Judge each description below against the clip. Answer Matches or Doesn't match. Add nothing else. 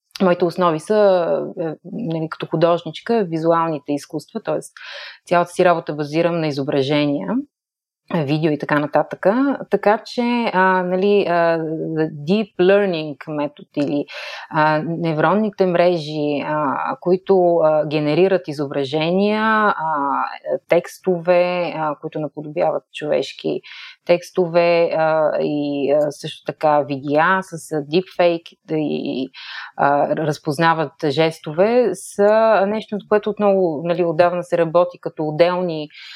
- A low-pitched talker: Doesn't match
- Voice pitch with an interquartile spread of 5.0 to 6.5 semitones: Doesn't match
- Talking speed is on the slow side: Matches